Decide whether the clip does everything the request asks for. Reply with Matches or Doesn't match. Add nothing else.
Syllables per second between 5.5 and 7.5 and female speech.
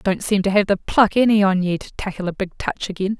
Matches